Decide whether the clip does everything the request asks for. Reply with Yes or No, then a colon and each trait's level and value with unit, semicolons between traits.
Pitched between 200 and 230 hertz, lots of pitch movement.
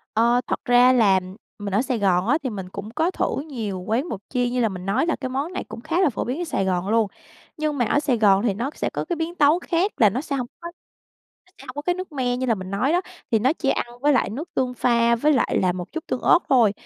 No: very high, 250 Hz; wide, 5.7 semitones